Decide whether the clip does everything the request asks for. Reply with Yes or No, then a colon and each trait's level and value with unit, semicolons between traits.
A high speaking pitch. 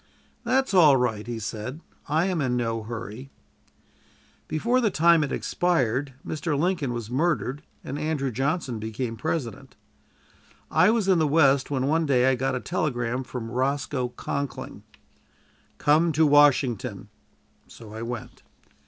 No: low, 135 Hz